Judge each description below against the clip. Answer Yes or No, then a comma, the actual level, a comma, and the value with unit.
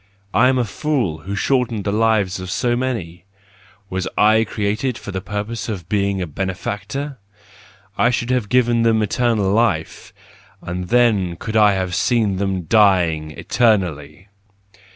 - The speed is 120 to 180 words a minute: Yes, average, 150 wpm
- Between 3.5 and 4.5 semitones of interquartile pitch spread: Yes, average, 4.0 semitones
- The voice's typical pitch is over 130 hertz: No, low, 105 Hz